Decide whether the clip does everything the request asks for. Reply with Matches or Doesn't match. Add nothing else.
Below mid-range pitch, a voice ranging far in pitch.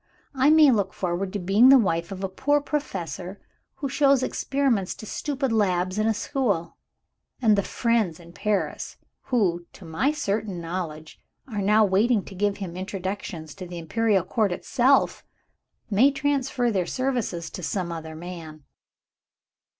Doesn't match